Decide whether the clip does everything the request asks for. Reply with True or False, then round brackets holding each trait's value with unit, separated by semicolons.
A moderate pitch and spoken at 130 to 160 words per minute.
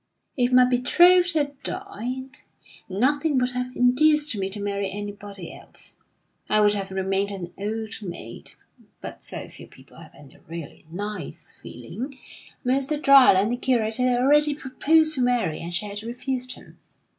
False (245 Hz; 155 wpm)